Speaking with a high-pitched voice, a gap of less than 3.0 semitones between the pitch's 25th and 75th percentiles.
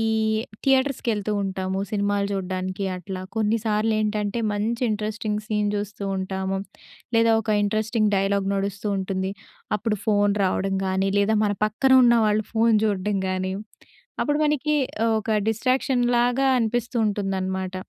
Yes: high, 210 Hz; narrow, 2.5 semitones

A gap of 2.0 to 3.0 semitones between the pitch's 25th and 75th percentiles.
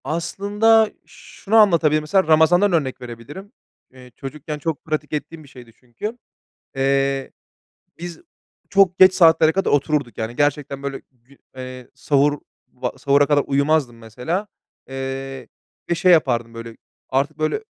No: average, 4.0 semitones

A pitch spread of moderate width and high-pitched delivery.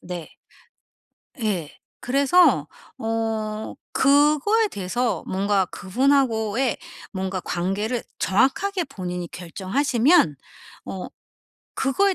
No: wide, 6.5 semitones; high, 225 Hz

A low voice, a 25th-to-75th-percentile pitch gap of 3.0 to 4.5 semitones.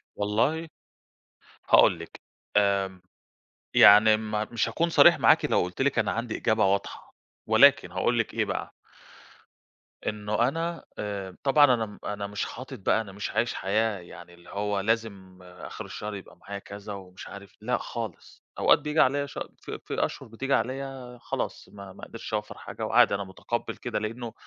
Yes: low, 105 Hz; average, 3.3 semitones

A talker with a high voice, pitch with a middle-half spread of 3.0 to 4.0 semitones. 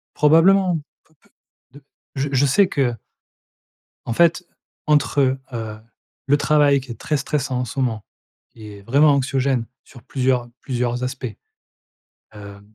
No: low, 135 Hz; average, 3.3 semitones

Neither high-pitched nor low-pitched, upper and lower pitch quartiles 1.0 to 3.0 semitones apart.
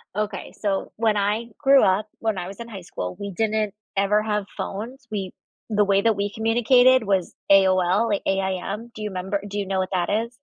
No: high, 205 Hz; narrow, 2.4 semitones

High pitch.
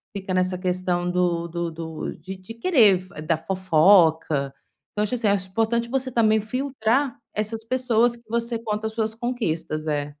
Yes: high, 200 Hz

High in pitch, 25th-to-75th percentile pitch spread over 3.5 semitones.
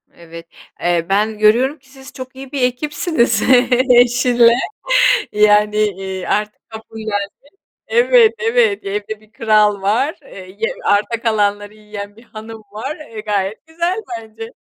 Yes: high, 220 Hz; average, 4.0 semitones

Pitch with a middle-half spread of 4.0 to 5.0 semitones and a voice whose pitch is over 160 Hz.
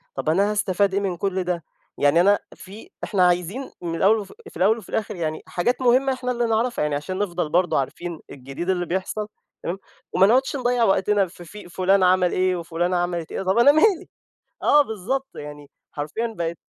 Yes: average, 4.3 semitones; medium, 185 Hz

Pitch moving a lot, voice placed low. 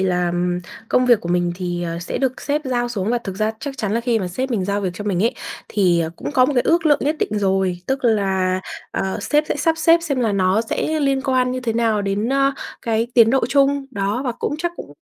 No: wide, 5.7 semitones; high, 225 Hz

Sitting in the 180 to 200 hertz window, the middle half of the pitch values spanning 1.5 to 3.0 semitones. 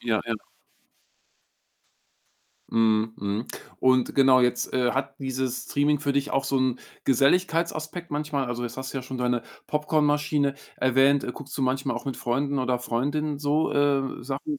No: low, 135 Hz; narrow, 2.5 semitones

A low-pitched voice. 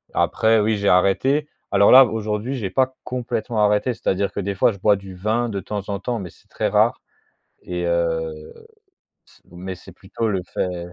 Yes: low, 100 Hz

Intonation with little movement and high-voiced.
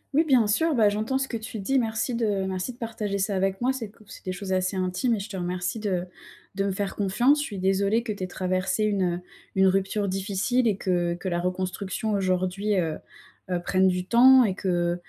No: average, 3.2 semitones; high, 195 Hz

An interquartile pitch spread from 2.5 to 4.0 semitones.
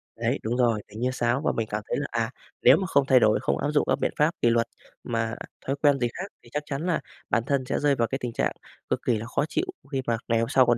Yes: average, 3.5 semitones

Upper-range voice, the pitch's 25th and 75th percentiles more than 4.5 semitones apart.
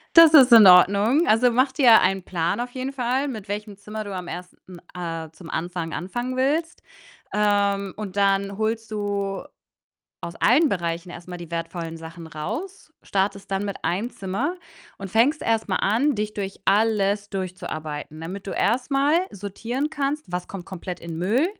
Yes: high, 200 Hz; average, 5.1 semitones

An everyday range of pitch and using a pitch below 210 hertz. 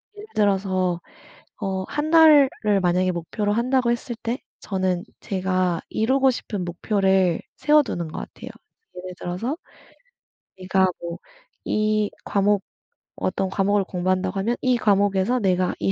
Yes: average, 4.1 semitones; high, 195 Hz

